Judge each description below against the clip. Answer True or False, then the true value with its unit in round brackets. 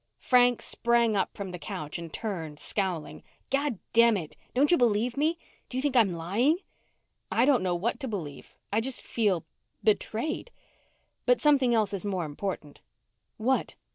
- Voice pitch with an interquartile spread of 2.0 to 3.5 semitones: False (5.5 semitones)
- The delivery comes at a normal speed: True (160 wpm)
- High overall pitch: True (220 Hz)